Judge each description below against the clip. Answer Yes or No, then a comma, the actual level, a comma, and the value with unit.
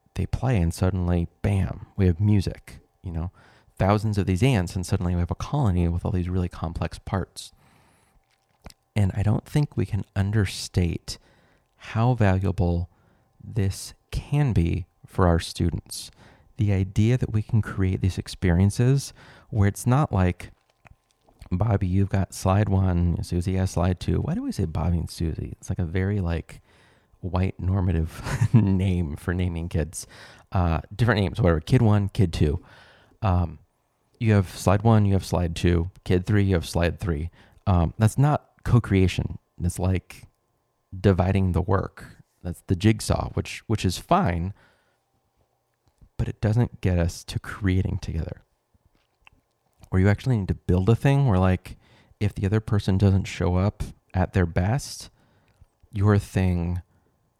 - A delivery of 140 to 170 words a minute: Yes, average, 155 wpm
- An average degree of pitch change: Yes, average, 3.6 semitones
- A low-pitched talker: Yes, very low, 95 Hz